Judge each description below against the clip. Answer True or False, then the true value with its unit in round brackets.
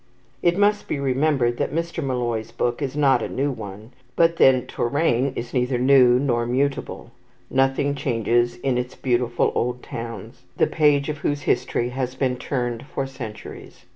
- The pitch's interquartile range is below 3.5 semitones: True (2.8 semitones)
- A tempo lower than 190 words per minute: True (165 wpm)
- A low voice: True (130 Hz)